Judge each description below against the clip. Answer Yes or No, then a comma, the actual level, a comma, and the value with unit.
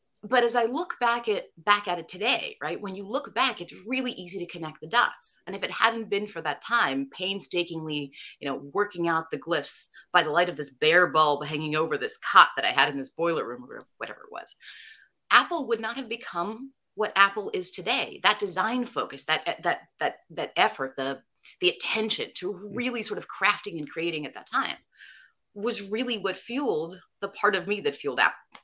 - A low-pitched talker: No, high, 200 Hz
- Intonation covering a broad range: Yes, wide, 6.5 semitones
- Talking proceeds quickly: Yes, fast, 210 wpm